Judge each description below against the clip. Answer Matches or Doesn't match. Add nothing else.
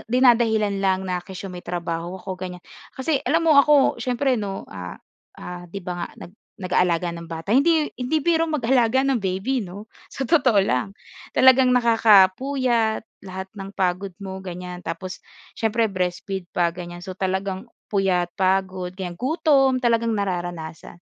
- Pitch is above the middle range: Matches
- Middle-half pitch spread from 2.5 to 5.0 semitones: Doesn't match